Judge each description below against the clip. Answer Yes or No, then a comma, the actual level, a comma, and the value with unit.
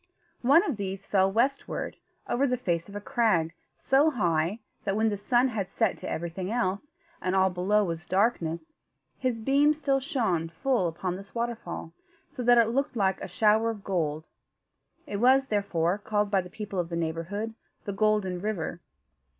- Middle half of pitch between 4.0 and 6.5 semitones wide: Yes, average, 4.9 semitones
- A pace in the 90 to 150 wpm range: No, average, 175 wpm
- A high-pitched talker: Yes, high, 205 Hz